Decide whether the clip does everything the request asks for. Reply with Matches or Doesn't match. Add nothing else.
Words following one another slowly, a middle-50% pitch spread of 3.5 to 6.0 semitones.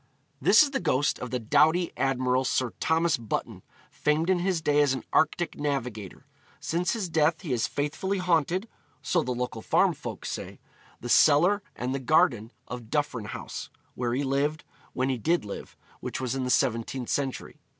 Doesn't match